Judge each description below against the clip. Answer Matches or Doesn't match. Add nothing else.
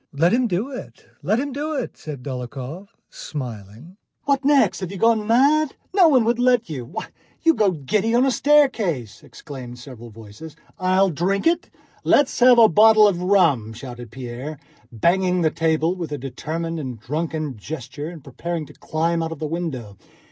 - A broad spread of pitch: Matches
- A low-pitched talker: Doesn't match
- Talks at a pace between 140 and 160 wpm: Doesn't match